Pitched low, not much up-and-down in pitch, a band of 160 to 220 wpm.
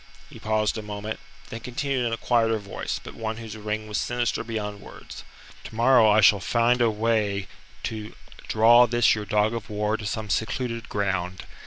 Yes: low, 110 Hz; narrow, 1.8 semitones; average, 180 wpm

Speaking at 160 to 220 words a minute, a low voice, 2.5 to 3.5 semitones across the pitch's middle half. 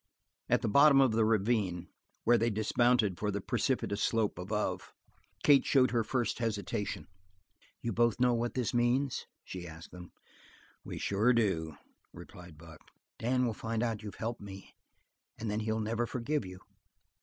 Yes: average, 165 wpm; low, 110 Hz; average, 3.1 semitones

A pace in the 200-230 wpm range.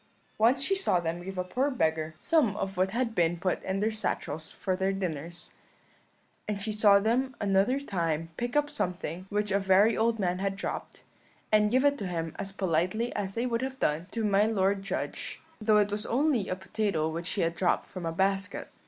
Yes: fast, 205 wpm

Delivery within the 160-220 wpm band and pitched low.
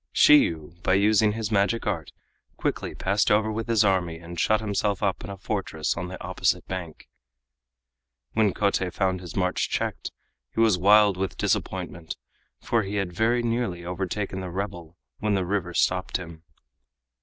Yes: average, 165 wpm; very low, 95 Hz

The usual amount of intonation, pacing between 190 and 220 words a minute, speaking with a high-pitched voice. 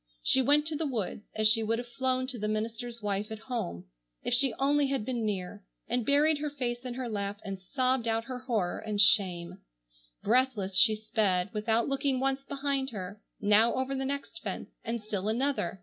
Yes: average, 4.1 semitones; average, 195 wpm; high, 235 Hz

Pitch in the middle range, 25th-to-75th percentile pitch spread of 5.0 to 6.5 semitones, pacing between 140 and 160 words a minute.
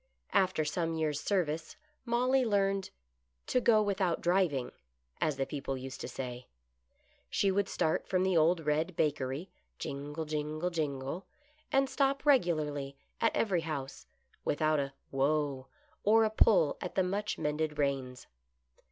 Yes: medium, 160 Hz; wide, 5.5 semitones; average, 150 wpm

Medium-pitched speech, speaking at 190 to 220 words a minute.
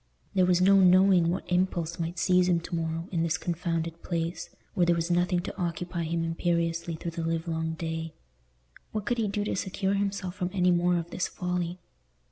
Yes: medium, 175 Hz; average, 195 wpm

